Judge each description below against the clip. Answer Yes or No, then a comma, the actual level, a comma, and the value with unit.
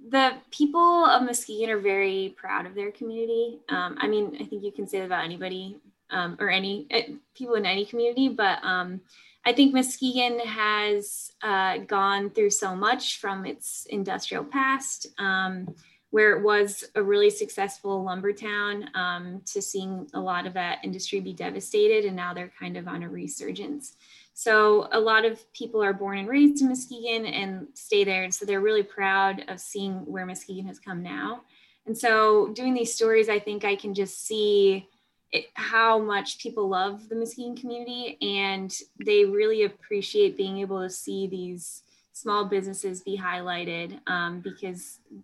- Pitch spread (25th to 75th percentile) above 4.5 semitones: No, average, 3.8 semitones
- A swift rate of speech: No, average, 175 wpm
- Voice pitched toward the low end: No, high, 205 Hz